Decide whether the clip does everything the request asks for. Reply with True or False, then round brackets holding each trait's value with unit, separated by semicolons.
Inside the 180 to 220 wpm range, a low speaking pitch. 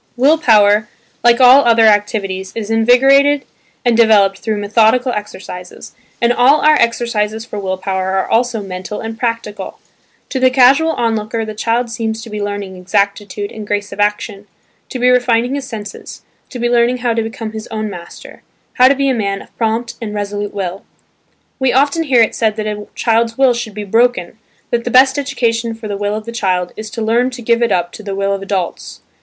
False (200 wpm; 225 Hz)